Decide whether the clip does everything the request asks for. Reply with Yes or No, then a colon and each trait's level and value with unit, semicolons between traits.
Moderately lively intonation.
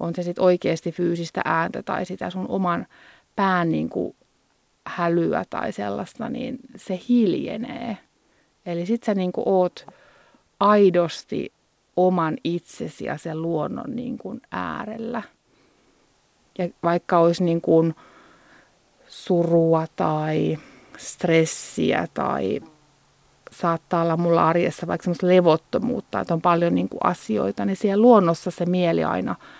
Yes: average, 3.8 semitones